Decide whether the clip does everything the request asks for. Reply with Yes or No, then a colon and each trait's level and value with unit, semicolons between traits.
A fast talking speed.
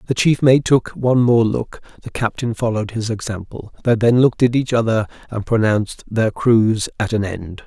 No: average, 190 wpm